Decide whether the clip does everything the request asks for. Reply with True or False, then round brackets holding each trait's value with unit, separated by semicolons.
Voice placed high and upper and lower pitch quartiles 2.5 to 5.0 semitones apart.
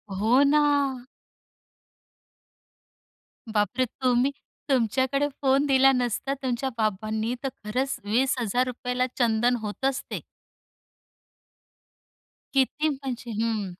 True (250 Hz; 3.0 semitones)